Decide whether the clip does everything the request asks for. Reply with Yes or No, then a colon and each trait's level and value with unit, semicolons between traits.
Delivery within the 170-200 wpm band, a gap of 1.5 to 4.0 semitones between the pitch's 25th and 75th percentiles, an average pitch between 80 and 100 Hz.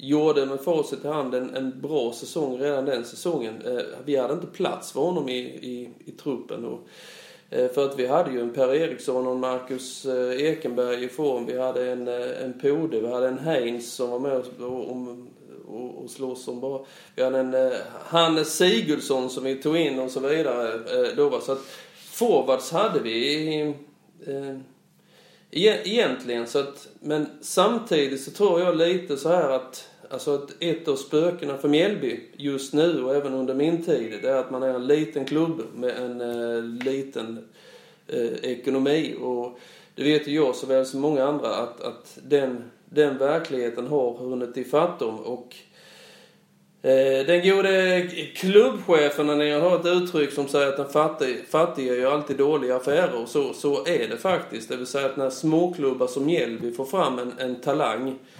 No: average, 185 wpm; average, 3.2 semitones; low, 135 Hz